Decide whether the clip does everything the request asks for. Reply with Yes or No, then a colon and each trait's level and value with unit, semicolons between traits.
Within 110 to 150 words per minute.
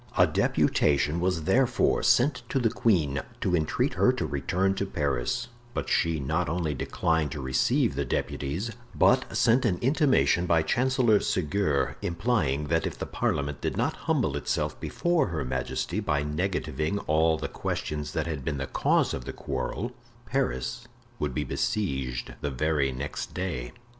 No: average, 160 wpm